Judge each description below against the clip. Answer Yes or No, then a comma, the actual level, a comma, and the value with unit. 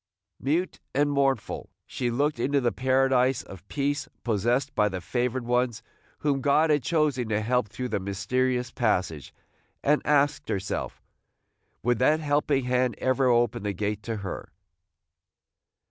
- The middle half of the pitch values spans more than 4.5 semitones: No, average, 3.9 semitones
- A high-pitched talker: No, low, 125 Hz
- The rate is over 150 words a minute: No, average, 145 wpm